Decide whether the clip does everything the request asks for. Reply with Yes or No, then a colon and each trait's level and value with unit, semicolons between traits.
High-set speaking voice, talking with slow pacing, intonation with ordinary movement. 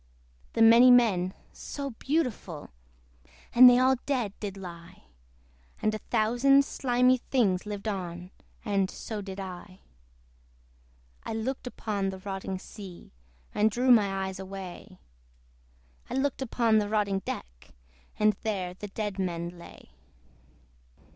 Yes: high, 205 Hz; slow, 130 wpm; average, 4.2 semitones